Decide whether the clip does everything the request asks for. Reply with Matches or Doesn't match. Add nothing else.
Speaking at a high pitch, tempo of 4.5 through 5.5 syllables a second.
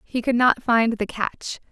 Doesn't match